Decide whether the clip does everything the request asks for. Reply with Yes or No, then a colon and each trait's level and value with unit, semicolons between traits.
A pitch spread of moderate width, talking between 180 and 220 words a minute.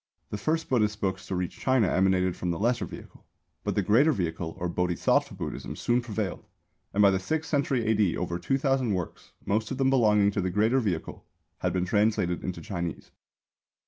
Yes: average, 4.9 semitones; average, 190 wpm